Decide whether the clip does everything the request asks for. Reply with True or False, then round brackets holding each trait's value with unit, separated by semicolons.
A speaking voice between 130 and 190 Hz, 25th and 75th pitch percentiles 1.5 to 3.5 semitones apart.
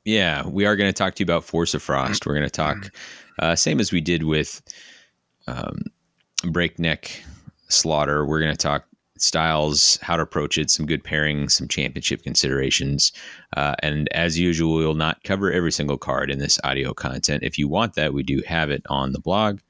False (75 Hz; 2.6 semitones)